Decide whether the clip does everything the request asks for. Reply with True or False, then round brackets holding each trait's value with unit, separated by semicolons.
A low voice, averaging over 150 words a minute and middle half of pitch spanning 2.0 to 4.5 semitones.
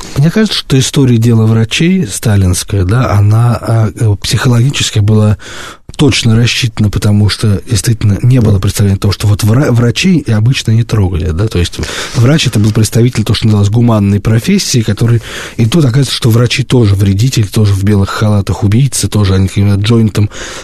True (110 Hz; 160 wpm; 2.8 semitones)